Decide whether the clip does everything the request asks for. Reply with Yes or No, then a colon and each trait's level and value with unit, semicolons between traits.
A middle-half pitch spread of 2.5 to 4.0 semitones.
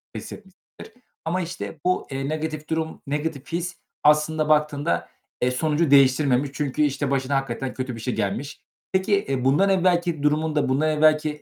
Yes: average, 2.9 semitones